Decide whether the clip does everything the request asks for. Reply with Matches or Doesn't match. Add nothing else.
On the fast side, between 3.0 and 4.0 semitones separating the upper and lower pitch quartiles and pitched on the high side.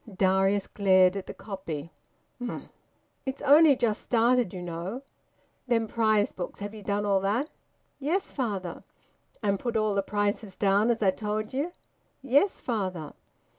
Doesn't match